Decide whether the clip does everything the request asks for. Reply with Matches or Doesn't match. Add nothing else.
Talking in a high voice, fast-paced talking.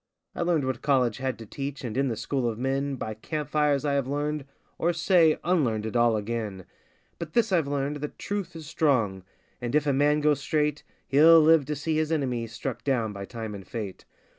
Doesn't match